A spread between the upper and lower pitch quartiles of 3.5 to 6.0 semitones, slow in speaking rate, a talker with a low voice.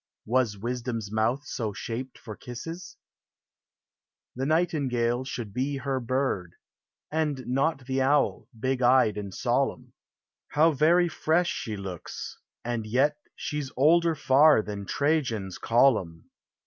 Yes: average, 4.5 semitones; slow, 120 wpm; low, 130 Hz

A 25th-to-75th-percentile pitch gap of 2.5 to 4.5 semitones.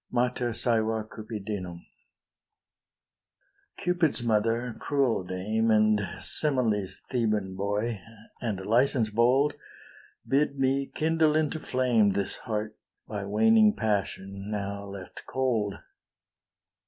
Yes: average, 4.1 semitones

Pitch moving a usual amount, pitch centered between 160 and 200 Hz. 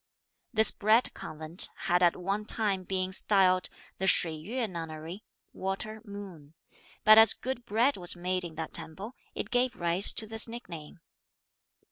Yes: average, 4.1 semitones; high, 190 Hz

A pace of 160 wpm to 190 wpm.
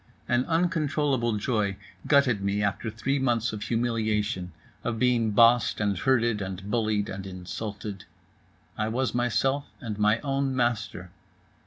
No: slow, 135 wpm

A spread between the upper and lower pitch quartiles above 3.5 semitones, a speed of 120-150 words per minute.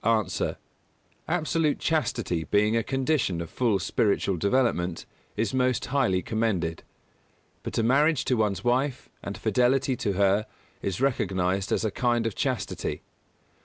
Yes: average, 4.9 semitones; average, 140 wpm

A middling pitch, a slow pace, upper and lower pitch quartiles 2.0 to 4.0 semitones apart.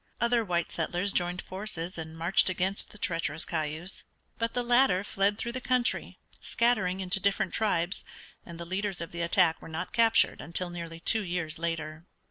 No: medium, 180 Hz; average, 175 wpm; average, 3.6 semitones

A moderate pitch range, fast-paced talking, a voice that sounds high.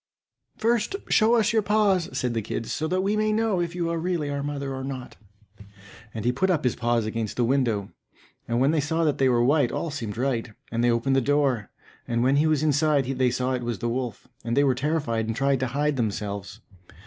No: average, 5.0 semitones; fast, 230 wpm; low, 135 Hz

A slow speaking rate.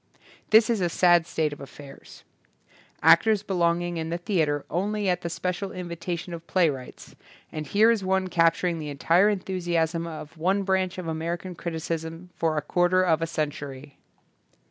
No: average, 165 wpm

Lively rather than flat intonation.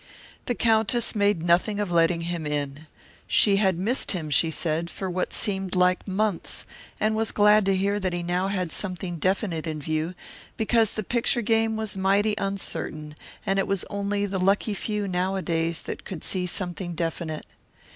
No: average, 3.2 semitones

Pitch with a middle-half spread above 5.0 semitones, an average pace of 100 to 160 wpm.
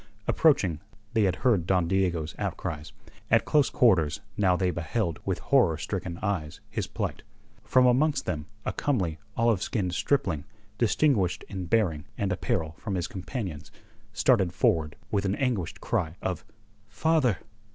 Yes: wide, 5.4 semitones; average, 145 wpm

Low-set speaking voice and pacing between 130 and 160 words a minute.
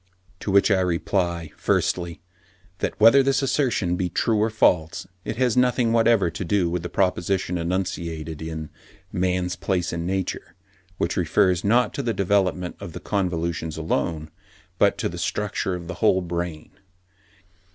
Yes: very low, 90 Hz; average, 155 wpm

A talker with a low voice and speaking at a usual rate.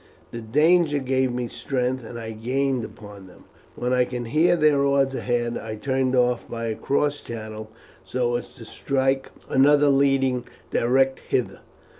Yes: low, 130 Hz; average, 160 wpm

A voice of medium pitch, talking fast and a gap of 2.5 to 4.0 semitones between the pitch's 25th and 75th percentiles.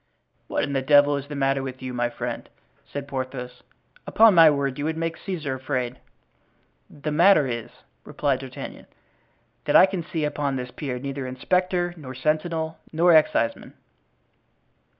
No: medium, 145 Hz; average, 155 wpm; average, 3.6 semitones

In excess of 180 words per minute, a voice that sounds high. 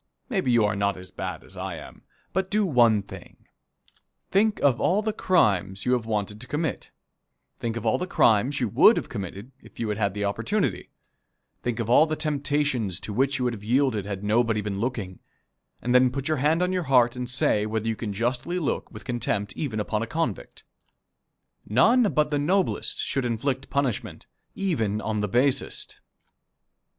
No: average, 190 wpm; low, 120 Hz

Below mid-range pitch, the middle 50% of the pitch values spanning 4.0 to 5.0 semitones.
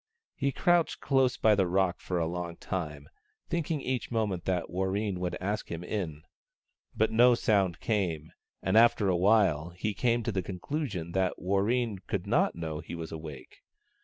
Yes: very low, 95 Hz; average, 4.6 semitones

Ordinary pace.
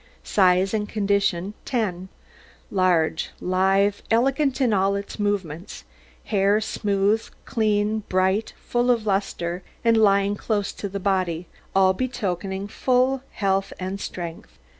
No: slow, 120 wpm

